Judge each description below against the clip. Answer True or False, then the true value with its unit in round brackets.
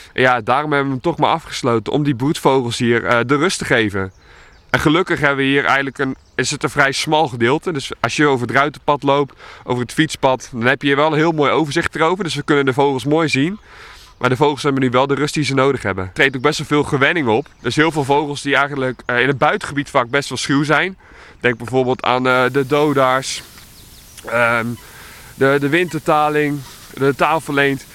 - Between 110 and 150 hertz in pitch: True (140 Hz)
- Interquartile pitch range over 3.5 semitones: False (2.8 semitones)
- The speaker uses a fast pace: True (225 wpm)